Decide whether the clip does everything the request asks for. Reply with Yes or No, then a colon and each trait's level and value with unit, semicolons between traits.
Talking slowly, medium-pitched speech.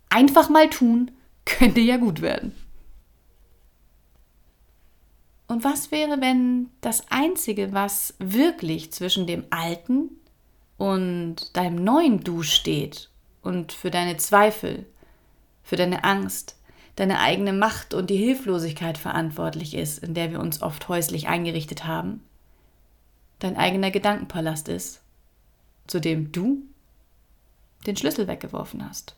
Yes: slow, 115 wpm; medium, 175 Hz